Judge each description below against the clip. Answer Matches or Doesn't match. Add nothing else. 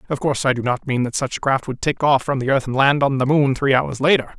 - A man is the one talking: Matches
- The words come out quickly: Matches